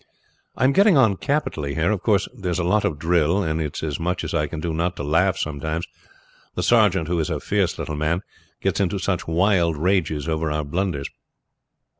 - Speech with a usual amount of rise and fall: Yes, average, 3.7 semitones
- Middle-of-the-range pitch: No, very low, 85 Hz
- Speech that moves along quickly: Yes, fast, 215 wpm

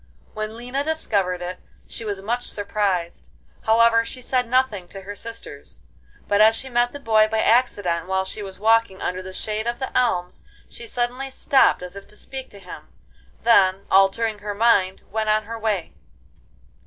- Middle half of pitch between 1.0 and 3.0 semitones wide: No, average, 3.5 semitones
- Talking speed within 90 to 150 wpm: No, average, 180 wpm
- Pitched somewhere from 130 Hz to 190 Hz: No, high, 215 Hz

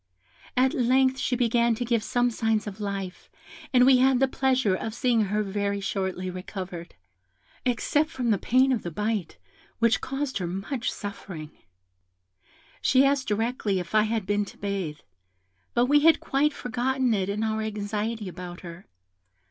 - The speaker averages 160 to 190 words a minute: Yes, average, 165 wpm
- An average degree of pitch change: Yes, average, 4.3 semitones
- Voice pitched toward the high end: Yes, high, 220 Hz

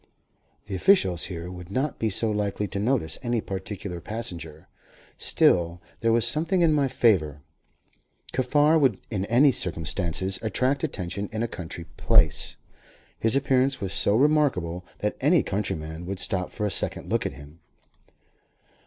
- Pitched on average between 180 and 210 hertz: No, low, 105 Hz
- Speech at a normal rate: Yes, average, 150 wpm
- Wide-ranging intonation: Yes, wide, 6.4 semitones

